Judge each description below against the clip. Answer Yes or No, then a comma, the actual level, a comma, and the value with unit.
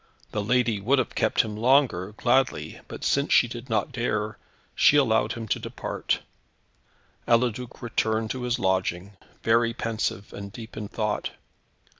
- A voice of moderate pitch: No, low, 115 Hz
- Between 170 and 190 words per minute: No, average, 150 wpm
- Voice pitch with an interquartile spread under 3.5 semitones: Yes, average, 2.7 semitones